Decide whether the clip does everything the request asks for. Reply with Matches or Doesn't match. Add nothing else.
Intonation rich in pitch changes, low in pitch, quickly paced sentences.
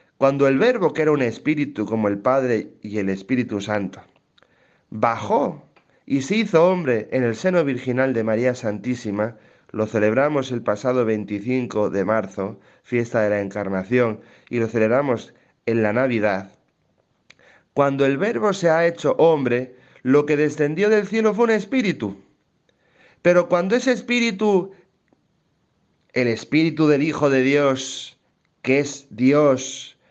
Doesn't match